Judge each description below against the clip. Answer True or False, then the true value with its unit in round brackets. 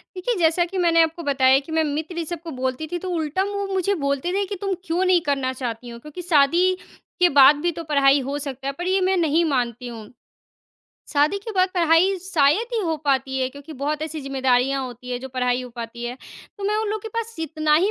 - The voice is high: True (310 Hz)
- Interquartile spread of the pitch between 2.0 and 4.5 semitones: False (5.2 semitones)